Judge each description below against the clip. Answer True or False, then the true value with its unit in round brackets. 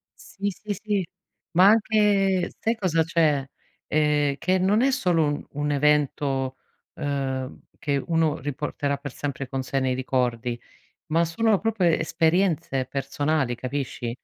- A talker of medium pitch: True (150 Hz)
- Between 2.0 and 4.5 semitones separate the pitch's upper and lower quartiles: False (5.2 semitones)